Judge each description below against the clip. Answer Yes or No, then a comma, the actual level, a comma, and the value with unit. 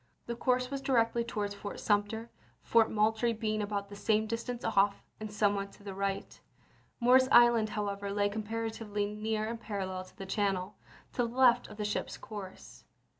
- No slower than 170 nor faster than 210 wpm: Yes, average, 175 wpm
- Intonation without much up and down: Yes, narrow, 2.2 semitones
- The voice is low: No, high, 215 Hz